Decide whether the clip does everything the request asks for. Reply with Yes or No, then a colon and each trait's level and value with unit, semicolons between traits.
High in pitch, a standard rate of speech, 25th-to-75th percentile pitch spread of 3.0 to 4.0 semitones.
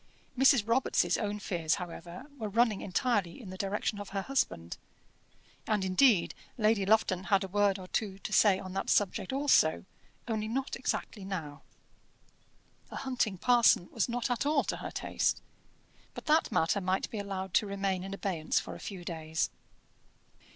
Yes: high, 200 Hz; average, 165 wpm; average, 3.7 semitones